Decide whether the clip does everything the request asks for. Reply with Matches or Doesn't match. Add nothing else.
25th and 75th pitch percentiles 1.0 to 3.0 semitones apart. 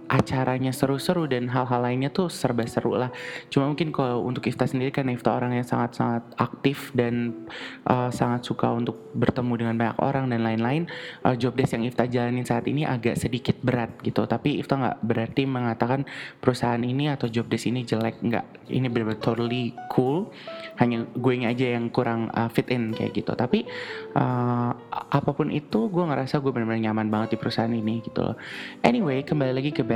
Matches